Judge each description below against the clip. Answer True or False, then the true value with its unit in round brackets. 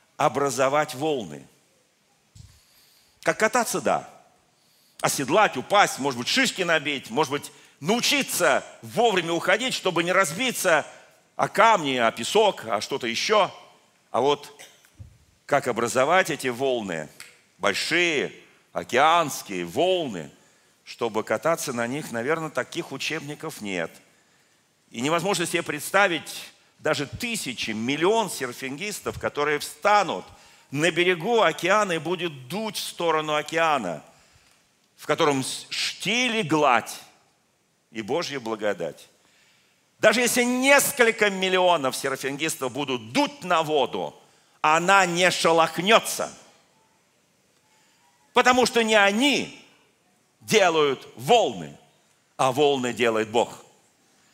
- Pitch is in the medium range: True (160 Hz)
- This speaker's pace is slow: True (100 wpm)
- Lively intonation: True (7.0 semitones)